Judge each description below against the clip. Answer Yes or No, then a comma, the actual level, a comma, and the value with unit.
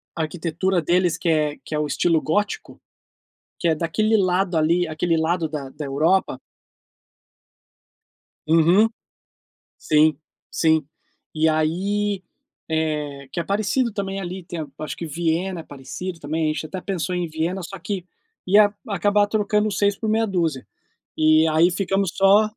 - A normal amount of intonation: Yes, average, 3.7 semitones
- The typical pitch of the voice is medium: Yes, medium, 170 Hz